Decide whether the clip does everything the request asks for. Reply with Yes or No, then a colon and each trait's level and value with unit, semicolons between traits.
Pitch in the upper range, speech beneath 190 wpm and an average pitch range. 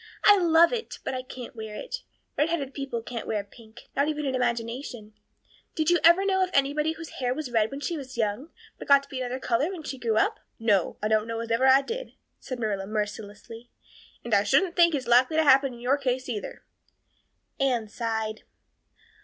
No: very high, 255 Hz; fast, 205 wpm; average, 4.8 semitones